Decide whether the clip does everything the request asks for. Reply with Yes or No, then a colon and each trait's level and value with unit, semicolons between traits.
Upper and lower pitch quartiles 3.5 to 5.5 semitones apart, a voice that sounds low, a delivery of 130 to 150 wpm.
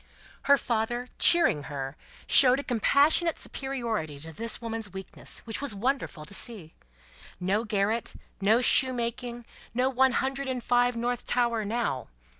No: average, 3.9 semitones; high, 235 Hz; average, 140 wpm